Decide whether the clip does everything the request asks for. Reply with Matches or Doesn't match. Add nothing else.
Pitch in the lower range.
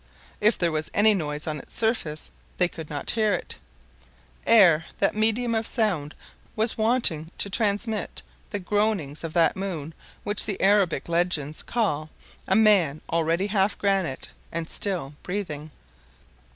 Doesn't match